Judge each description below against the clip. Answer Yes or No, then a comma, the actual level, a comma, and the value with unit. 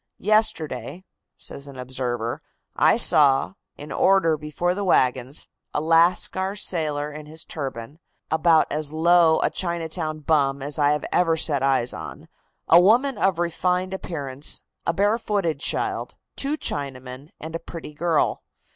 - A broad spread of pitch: No, average, 3.7 semitones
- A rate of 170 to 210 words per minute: No, average, 140 wpm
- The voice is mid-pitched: Yes, medium, 160 Hz